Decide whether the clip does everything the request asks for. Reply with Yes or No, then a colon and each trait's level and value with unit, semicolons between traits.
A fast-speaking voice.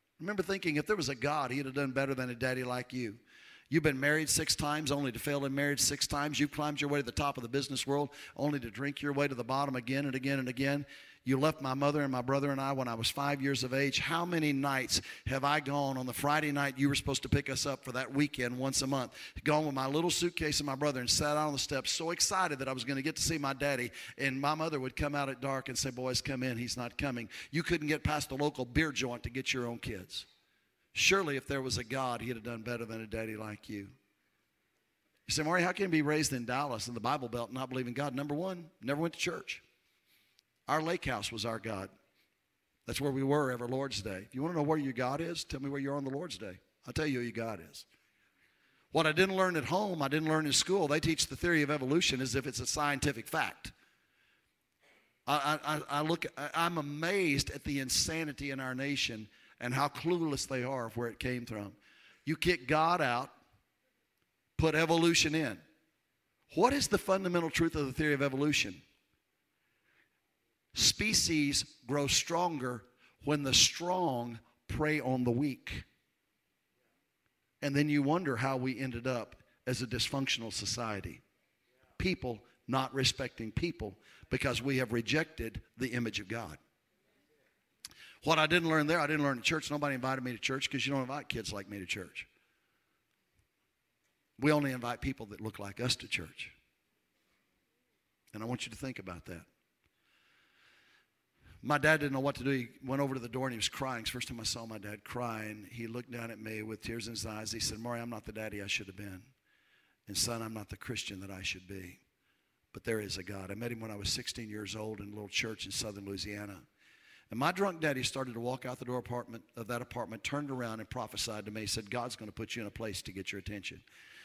Yes: fast, 230 wpm